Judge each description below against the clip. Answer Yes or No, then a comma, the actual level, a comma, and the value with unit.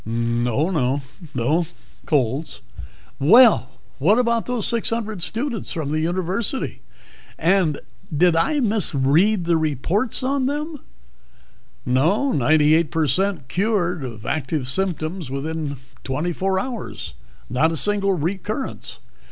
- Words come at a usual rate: No, slow, 115 wpm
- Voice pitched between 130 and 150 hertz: No, medium, 170 Hz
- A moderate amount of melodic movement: No, wide, 6.4 semitones